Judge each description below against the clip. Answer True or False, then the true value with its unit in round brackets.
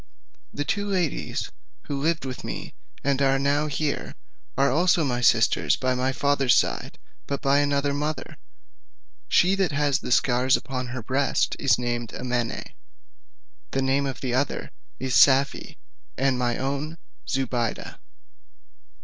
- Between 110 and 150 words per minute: True (140 wpm)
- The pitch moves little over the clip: True (2.0 semitones)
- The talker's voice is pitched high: False (135 Hz)